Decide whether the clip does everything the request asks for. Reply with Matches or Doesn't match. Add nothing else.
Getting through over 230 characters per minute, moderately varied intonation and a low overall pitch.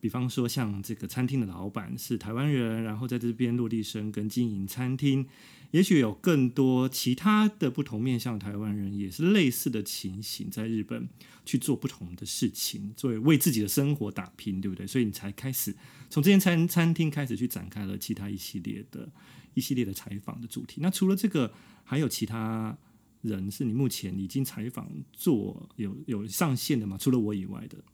Matches